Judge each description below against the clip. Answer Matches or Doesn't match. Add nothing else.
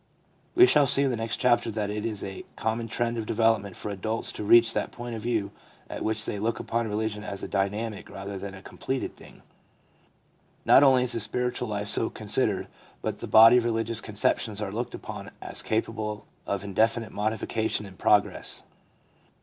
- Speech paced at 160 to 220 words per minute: Matches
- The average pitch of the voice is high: Doesn't match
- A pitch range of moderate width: Doesn't match